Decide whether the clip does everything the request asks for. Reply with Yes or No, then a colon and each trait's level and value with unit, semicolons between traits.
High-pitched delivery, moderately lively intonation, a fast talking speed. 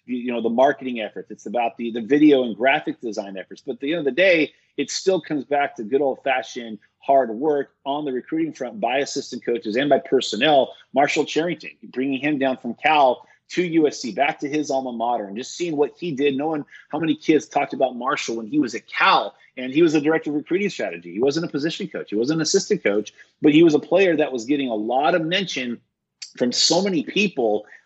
No: medium, 140 Hz; average, 3.8 semitones; fast, 230 wpm